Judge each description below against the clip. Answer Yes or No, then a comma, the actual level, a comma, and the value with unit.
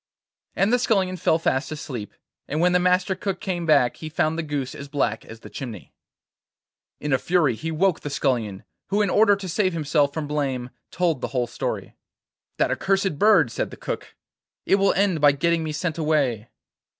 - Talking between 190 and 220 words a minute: Yes, average, 195 wpm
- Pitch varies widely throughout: No, average, 5.0 semitones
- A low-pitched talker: No, medium, 155 Hz